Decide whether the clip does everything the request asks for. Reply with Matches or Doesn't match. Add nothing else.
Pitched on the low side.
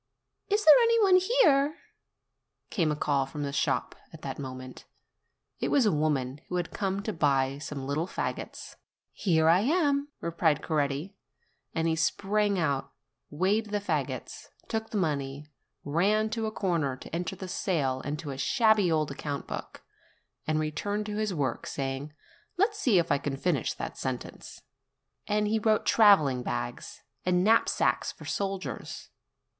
Doesn't match